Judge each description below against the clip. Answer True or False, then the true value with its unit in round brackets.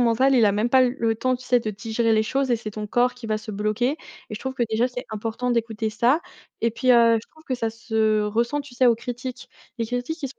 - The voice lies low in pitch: False (235 Hz)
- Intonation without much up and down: True (2.3 semitones)